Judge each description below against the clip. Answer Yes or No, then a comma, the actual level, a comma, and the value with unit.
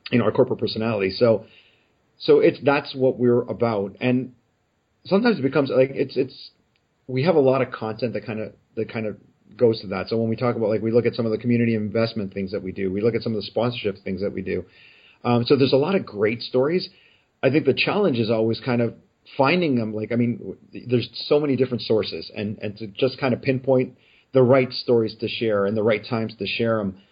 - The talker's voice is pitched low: Yes, low, 115 Hz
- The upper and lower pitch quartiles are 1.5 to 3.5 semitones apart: Yes, average, 3.1 semitones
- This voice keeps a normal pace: No, fast, 240 wpm